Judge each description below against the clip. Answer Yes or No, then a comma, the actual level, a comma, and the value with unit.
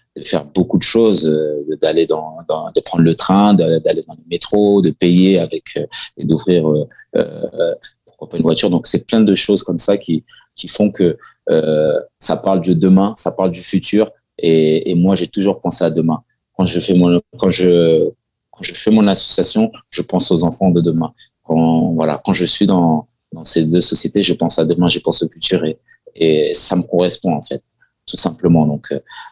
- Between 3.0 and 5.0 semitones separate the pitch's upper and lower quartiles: Yes, average, 3.8 semitones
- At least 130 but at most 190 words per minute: No, average, 210 wpm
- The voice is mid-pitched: No, very low, 90 Hz